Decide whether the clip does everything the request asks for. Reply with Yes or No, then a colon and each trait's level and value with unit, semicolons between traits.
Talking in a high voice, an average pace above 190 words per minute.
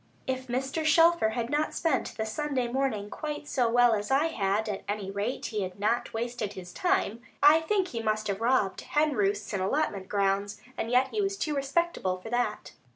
Yes: high, 240 Hz; average, 200 wpm